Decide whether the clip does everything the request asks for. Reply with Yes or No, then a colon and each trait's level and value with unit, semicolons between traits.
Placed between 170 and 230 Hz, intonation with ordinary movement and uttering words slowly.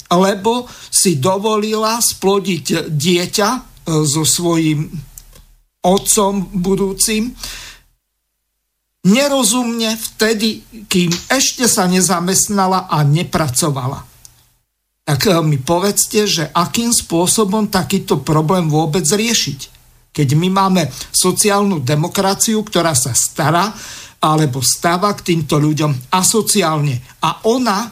Yes: medium, 185 Hz; average, 4.9 semitones; slow, 90 wpm